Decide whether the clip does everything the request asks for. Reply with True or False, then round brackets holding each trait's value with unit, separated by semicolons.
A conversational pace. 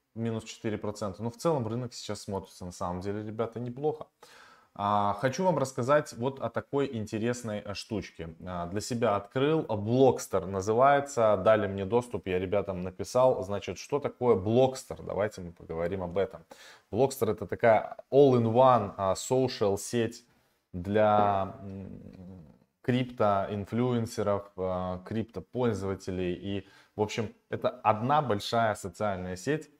True (135 wpm)